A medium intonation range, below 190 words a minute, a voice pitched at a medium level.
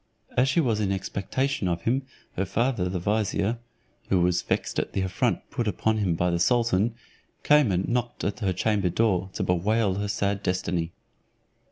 No: average, 4.1 semitones; average, 180 wpm; low, 100 Hz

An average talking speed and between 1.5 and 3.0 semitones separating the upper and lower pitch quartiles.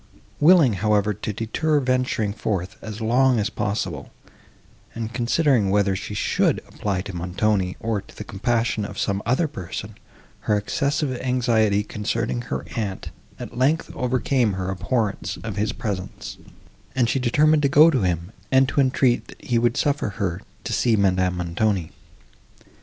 No: average, 155 wpm; average, 4.6 semitones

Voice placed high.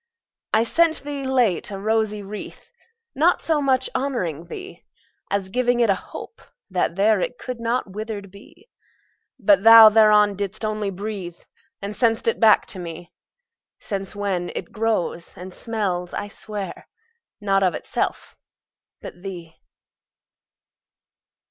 Yes: high, 210 Hz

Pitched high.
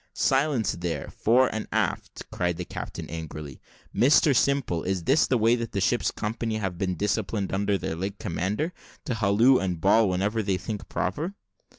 No: low, 100 Hz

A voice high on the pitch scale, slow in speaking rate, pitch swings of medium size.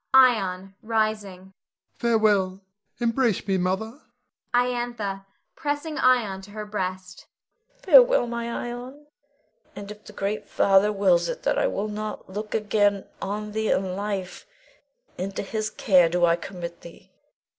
Yes: high, 210 Hz; slow, 130 wpm; average, 3.3 semitones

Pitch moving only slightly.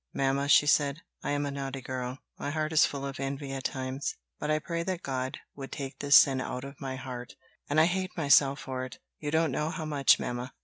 Yes: narrow, 2.3 semitones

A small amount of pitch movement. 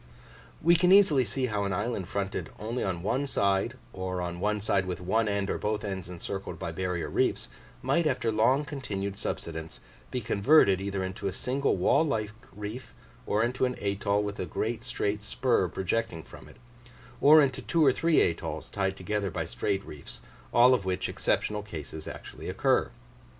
No: average, 4.8 semitones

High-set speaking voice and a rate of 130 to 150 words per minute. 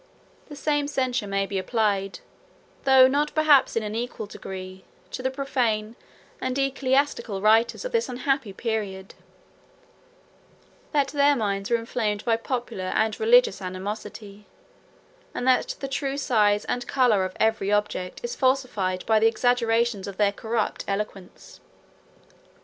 Yes: high, 225 Hz; average, 140 wpm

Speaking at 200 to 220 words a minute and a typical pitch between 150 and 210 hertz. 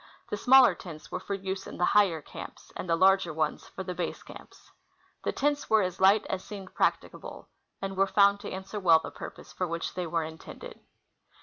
Yes: fast, 205 wpm; high, 190 Hz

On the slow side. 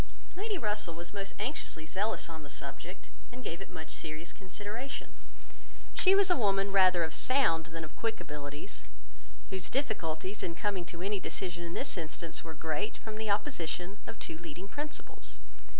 No: average, 170 wpm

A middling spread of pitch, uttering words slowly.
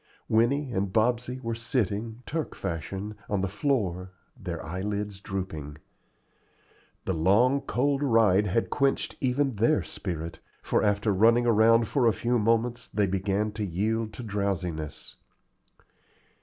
Yes: average, 3.8 semitones; slow, 130 wpm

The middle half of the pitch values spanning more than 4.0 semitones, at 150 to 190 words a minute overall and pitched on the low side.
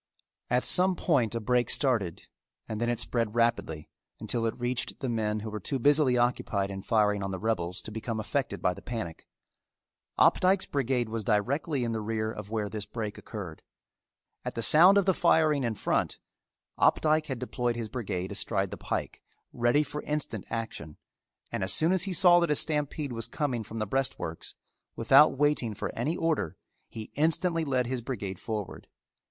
Yes: average, 5.1 semitones; average, 180 wpm; low, 120 Hz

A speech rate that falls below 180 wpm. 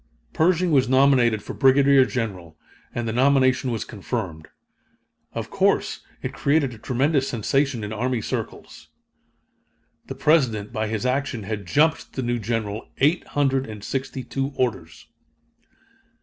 Yes: slow, 135 wpm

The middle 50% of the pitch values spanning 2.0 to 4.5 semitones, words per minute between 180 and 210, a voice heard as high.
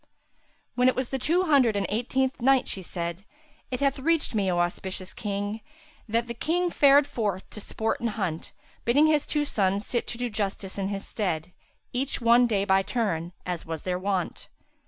No: average, 5.2 semitones; average, 190 wpm; high, 220 Hz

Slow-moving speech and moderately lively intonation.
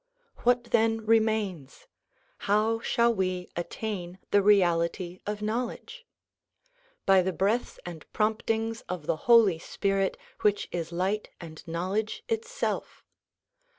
Yes: slow, 120 wpm; average, 3.8 semitones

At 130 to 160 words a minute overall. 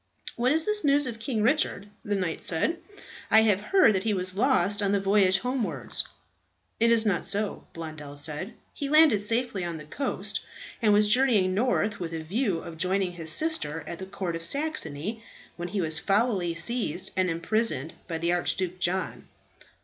No: average, 180 wpm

